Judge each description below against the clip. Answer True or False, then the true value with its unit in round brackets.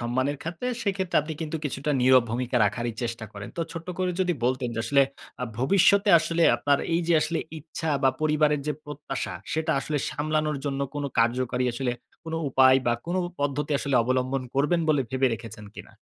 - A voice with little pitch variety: False (3.8 semitones)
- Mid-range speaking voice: True (145 Hz)